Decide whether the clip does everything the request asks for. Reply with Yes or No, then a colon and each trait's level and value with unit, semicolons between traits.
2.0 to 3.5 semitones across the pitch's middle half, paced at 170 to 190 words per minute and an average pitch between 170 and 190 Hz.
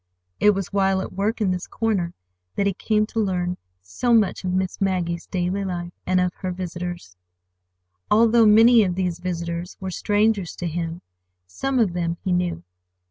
Yes: average, 2.8 semitones; average, 175 wpm; medium, 185 Hz